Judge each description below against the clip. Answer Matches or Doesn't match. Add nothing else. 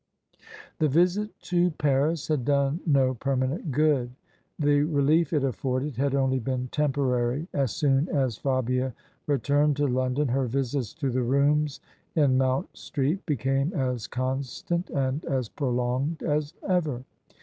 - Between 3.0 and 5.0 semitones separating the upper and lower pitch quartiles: Doesn't match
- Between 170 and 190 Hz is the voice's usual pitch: Doesn't match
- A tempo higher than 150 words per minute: Doesn't match